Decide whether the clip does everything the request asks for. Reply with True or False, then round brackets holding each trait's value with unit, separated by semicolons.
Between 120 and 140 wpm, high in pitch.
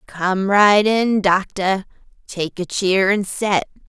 True (135 wpm; 195 Hz)